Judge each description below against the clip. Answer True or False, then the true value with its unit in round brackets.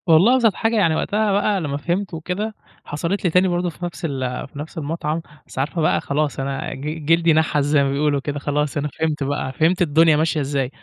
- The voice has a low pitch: False (155 Hz)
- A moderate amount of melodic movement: True (3.4 semitones)